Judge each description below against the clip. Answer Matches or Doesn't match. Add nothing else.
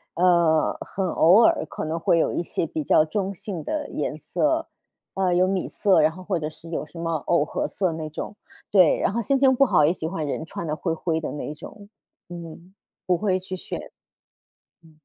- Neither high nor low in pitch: Matches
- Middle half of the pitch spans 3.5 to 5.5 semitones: Doesn't match